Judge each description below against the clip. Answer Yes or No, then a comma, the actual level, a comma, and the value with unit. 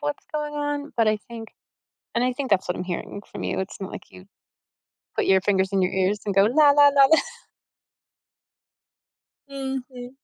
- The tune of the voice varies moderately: No, wide, 6.5 semitones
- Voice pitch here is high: Yes, high, 245 Hz